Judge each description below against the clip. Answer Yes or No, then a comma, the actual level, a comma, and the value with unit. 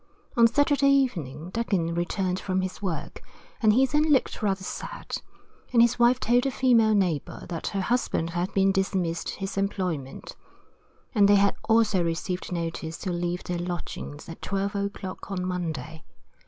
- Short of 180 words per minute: Yes, average, 160 wpm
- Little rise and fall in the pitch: No, average, 4.6 semitones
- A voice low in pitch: No, high, 190 Hz